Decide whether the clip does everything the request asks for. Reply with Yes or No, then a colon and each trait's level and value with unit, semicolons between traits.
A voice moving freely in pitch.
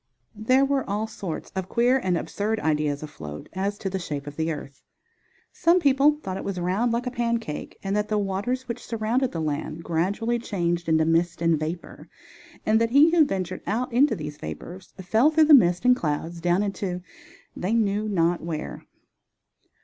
Yes: wide, 5.9 semitones